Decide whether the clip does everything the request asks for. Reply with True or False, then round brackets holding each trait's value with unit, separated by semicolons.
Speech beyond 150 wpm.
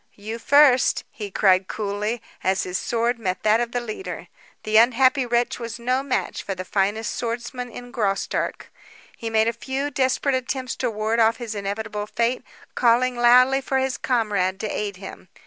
True (175 wpm)